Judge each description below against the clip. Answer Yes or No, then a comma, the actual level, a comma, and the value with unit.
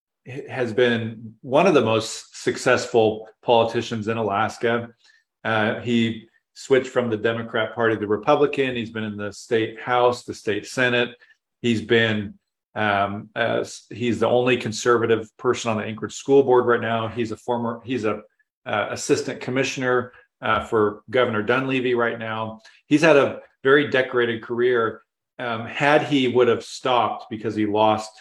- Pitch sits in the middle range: No, low, 115 Hz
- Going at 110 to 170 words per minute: Yes, average, 155 wpm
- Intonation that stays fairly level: Yes, narrow, 2.2 semitones